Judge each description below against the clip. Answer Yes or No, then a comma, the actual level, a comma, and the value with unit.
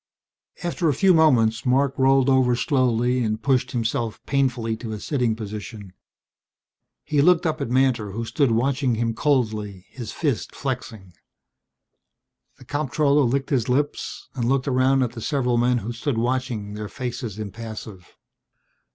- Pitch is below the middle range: Yes, low, 125 Hz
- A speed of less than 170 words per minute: Yes, average, 150 wpm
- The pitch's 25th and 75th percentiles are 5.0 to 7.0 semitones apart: No, average, 3.3 semitones